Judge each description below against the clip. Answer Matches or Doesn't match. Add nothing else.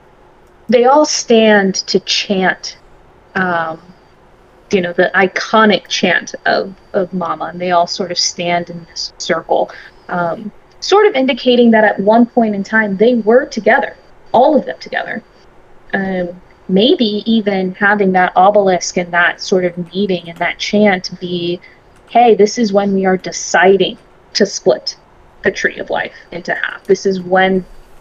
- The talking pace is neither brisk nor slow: Matches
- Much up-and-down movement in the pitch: Doesn't match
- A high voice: Matches